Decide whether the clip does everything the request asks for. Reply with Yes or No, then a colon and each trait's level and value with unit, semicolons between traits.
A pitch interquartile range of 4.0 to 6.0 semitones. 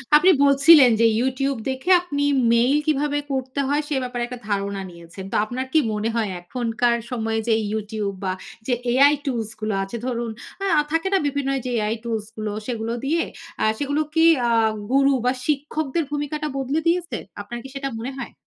Yes: average, 4.3 semitones